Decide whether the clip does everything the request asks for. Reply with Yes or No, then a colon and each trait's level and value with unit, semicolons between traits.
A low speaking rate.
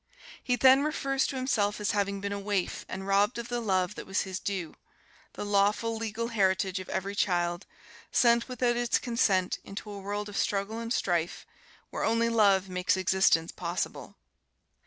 No: average, 175 wpm